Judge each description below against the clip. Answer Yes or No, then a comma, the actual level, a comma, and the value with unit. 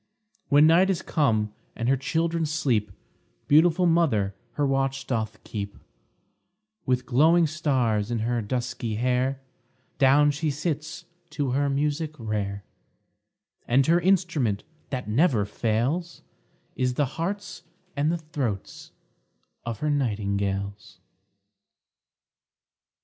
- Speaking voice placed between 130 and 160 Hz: Yes, low, 135 Hz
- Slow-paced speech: Yes, slow, 110 wpm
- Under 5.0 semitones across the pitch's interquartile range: No, wide, 5.6 semitones